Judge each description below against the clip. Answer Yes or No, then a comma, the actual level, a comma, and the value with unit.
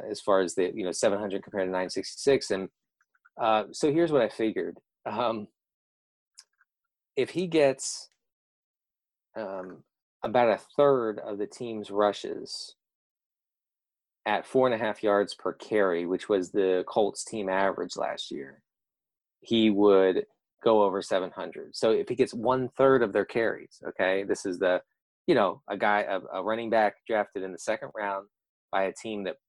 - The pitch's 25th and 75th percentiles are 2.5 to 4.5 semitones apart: No, average, 5.0 semitones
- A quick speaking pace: No, average, 165 wpm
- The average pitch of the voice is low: Yes, low, 105 Hz